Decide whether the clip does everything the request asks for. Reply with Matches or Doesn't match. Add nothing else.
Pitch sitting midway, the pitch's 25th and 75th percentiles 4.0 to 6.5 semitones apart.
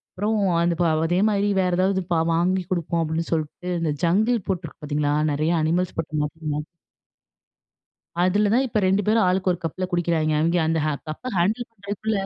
Doesn't match